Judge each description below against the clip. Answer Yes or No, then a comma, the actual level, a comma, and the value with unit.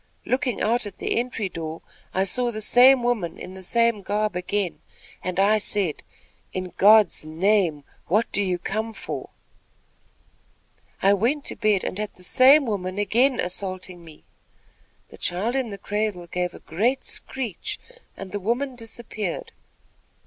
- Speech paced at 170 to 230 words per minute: No, average, 155 wpm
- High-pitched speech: Yes, high, 205 Hz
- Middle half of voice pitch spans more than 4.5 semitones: No, average, 4.2 semitones